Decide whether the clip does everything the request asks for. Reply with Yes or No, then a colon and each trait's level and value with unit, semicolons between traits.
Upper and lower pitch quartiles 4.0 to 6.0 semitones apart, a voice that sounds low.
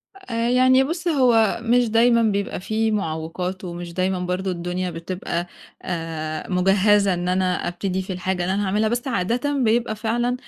No: average, 4.4 semitones; high, 195 Hz